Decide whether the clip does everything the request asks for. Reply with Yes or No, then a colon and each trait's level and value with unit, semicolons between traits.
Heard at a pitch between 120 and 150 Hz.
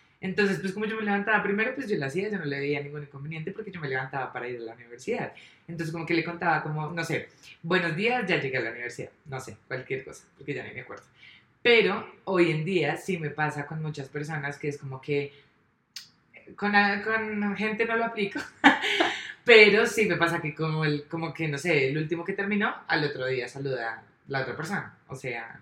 No: medium, 160 Hz